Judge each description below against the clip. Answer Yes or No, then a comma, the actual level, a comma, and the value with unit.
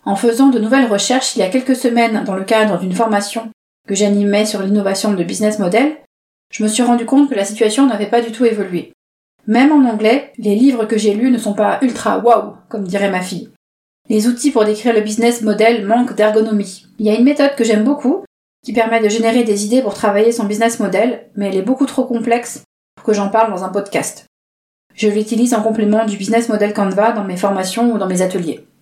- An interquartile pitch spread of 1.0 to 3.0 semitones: Yes, narrow, 2.4 semitones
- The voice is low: No, high, 220 Hz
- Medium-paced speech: No, fast, 225 wpm